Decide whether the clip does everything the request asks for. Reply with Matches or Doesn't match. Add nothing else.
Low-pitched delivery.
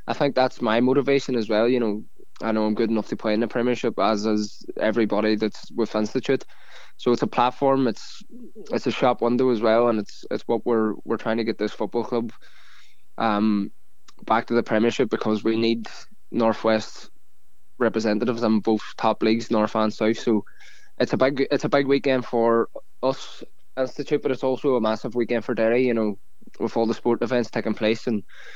Matches